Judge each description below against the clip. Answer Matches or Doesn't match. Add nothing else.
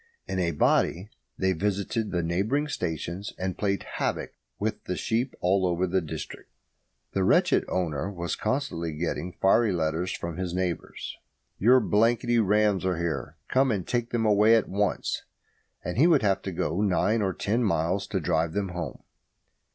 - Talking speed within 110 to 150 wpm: Doesn't match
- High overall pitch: Doesn't match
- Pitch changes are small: Doesn't match